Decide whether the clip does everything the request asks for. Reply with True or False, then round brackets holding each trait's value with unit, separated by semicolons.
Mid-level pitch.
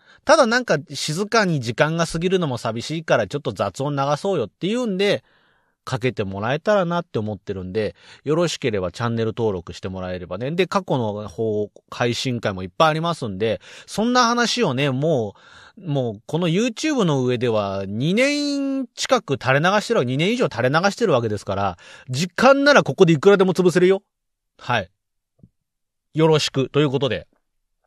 True (150 Hz)